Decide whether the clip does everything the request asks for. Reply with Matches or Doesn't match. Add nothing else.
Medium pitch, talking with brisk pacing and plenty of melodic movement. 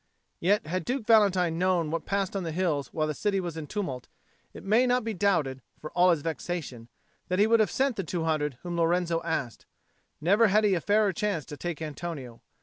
Doesn't match